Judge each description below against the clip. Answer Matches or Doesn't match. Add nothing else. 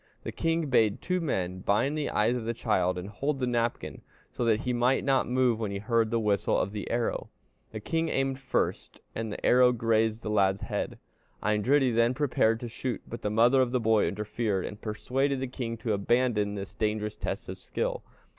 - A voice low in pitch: Matches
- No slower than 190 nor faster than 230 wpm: Matches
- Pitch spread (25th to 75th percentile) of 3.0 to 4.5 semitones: Matches